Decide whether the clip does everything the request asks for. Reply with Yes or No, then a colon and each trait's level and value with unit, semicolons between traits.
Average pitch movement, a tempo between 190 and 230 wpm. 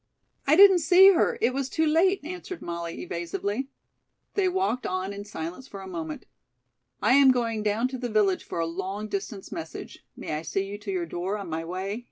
No: wide, 7.1 semitones; fast, 205 wpm